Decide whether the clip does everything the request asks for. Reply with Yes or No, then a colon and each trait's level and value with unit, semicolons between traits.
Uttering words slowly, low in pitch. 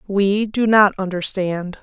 No: slow, 130 wpm; high, 195 Hz